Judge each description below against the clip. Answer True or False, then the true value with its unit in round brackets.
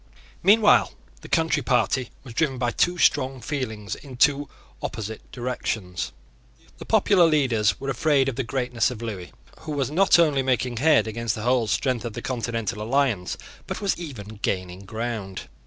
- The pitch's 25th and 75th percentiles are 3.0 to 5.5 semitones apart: True (4.2 semitones)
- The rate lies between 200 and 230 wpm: False (165 wpm)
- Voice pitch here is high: False (125 Hz)